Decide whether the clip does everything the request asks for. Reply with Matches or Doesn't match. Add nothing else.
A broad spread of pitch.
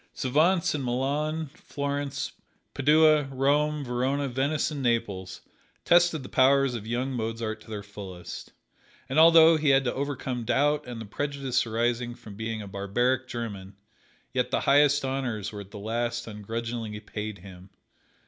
Doesn't match